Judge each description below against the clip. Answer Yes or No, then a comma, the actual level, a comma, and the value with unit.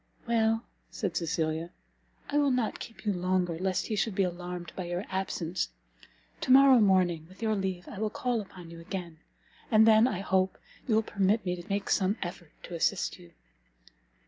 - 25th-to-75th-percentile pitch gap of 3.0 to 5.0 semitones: Yes, average, 3.7 semitones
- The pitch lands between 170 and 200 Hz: Yes, high, 190 Hz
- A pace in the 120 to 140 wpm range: No, average, 185 wpm